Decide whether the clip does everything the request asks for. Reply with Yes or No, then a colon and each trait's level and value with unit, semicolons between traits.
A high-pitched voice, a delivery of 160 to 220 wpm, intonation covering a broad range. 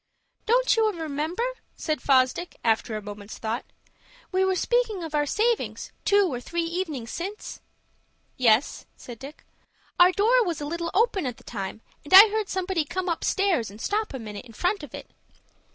Yes: very high, 335 Hz; average, 175 wpm; wide, 7.8 semitones